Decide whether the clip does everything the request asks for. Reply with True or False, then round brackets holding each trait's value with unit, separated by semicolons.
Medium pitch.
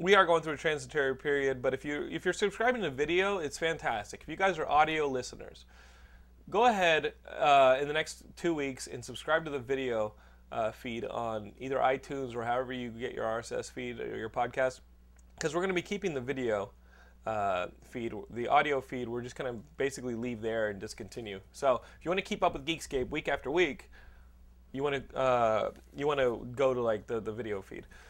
False (130 Hz)